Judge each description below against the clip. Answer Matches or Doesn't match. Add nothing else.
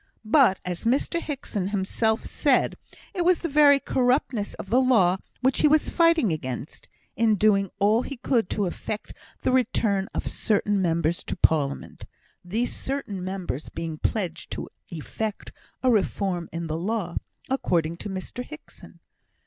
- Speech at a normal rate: Matches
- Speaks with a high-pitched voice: Matches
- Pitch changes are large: Matches